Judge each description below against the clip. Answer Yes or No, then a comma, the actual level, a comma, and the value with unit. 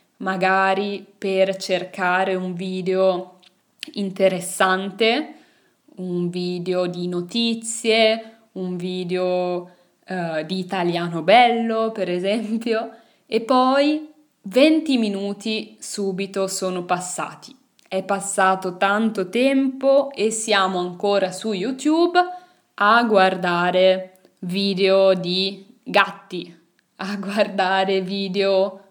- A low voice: No, high, 195 Hz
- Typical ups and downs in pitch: Yes, average, 3.3 semitones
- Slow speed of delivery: Yes, slow, 85 wpm